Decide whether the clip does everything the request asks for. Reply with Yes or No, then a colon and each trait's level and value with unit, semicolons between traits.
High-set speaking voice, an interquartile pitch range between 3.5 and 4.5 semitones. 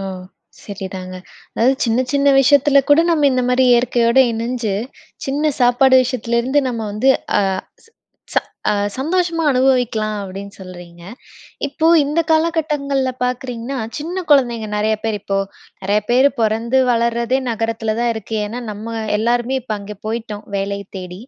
Yes: high, 235 Hz; average, 3.8 semitones